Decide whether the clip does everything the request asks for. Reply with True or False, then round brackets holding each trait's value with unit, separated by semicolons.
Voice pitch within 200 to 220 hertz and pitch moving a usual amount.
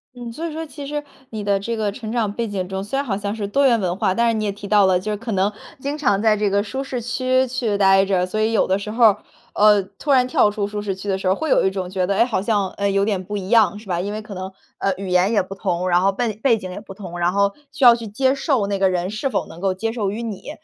True (205 Hz; 3.2 semitones)